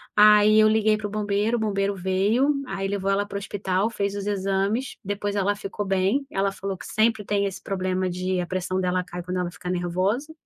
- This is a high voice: Yes, high, 200 Hz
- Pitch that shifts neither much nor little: No, narrow, 2.0 semitones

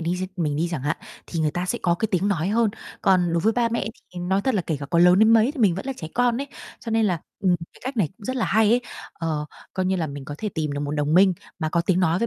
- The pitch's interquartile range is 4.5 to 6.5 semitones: Yes, average, 5.1 semitones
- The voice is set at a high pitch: No, medium, 180 Hz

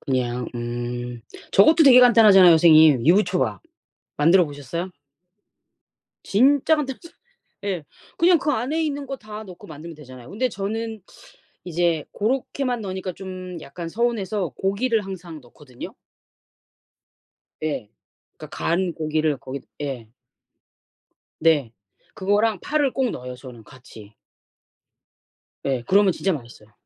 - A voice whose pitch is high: No, medium, 180 Hz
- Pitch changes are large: Yes, wide, 7.8 semitones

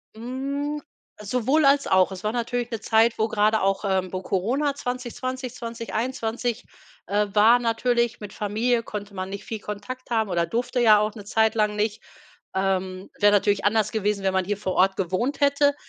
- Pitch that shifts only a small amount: No, average, 3.4 semitones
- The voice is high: Yes, high, 220 Hz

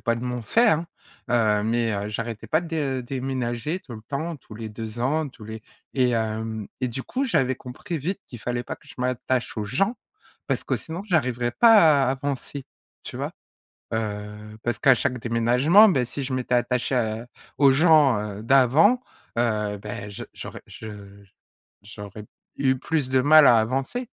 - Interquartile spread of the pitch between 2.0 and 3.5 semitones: No, average, 4.2 semitones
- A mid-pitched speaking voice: No, low, 125 Hz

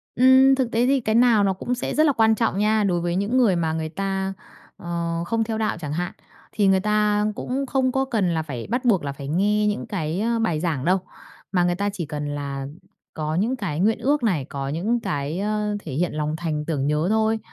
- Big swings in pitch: Yes, wide, 5.7 semitones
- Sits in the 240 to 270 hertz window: No, high, 195 Hz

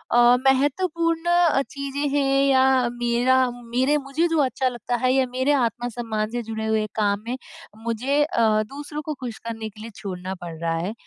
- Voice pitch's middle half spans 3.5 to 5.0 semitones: Yes, average, 3.9 semitones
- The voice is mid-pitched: No, very high, 250 Hz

